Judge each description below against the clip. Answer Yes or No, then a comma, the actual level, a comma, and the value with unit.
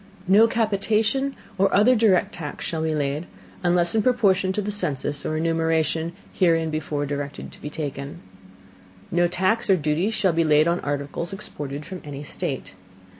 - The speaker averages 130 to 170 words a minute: Yes, average, 165 wpm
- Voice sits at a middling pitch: Yes, medium, 165 Hz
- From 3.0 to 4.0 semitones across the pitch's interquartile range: No, average, 4.8 semitones